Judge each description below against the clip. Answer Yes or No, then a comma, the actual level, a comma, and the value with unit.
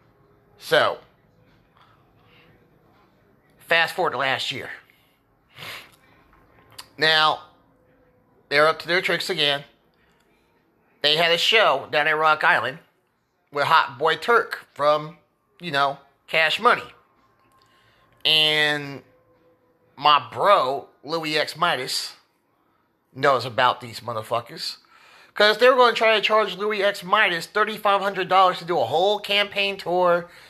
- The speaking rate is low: Yes, slow, 115 wpm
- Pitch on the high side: No, medium, 160 Hz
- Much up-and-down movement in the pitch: Yes, wide, 5.8 semitones